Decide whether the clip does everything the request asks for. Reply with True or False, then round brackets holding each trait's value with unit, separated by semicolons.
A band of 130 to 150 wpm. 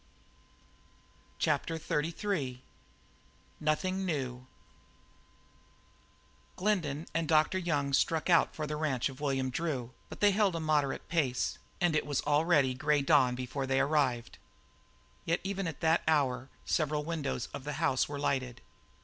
True (135 wpm)